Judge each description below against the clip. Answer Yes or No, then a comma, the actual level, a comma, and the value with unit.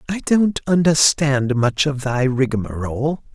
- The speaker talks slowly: Yes, slow, 125 wpm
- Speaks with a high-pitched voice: No, medium, 140 Hz